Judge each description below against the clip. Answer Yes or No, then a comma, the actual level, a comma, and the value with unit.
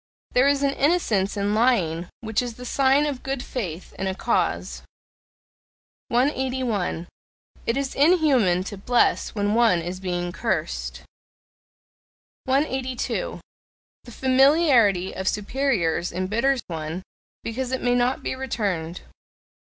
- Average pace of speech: No, slow, 120 wpm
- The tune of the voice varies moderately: No, wide, 6.0 semitones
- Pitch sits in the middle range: No, high, 240 Hz